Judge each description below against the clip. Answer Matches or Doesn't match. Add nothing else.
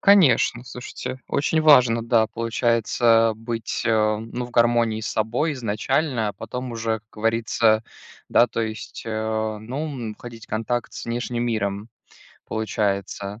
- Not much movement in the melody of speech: Matches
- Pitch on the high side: Doesn't match